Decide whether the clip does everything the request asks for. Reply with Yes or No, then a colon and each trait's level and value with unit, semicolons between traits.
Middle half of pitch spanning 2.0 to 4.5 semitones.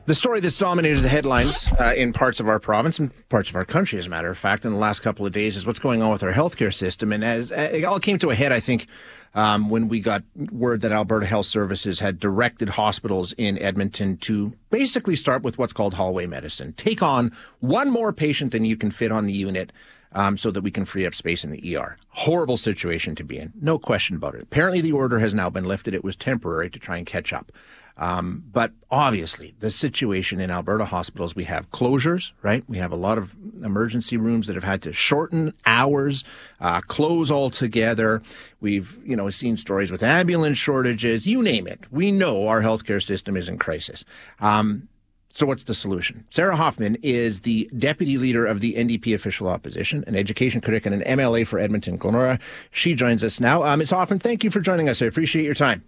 No: average, 5.3 semitones